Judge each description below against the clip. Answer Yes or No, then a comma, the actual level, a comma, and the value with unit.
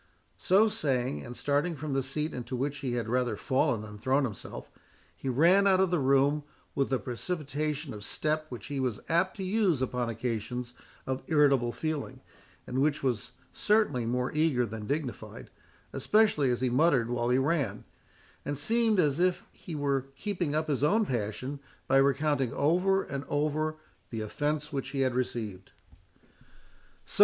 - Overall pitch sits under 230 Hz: Yes, medium, 140 Hz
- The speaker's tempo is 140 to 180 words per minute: Yes, average, 165 wpm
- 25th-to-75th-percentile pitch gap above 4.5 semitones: No, average, 3.8 semitones